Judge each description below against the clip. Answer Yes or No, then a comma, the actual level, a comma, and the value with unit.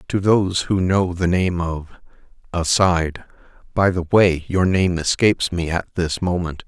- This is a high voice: No, very low, 90 Hz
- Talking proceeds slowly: No, average, 160 wpm